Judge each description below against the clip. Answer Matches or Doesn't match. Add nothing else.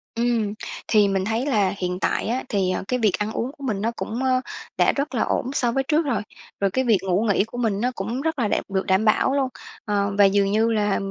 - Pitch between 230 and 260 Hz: Doesn't match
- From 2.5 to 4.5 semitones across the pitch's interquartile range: Matches